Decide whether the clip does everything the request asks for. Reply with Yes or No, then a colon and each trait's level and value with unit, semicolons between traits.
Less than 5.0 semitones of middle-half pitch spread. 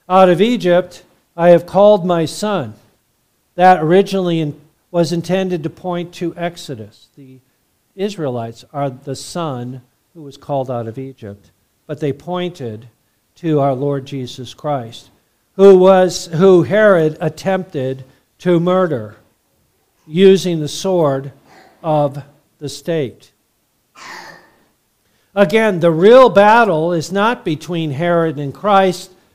No: wide, 5.4 semitones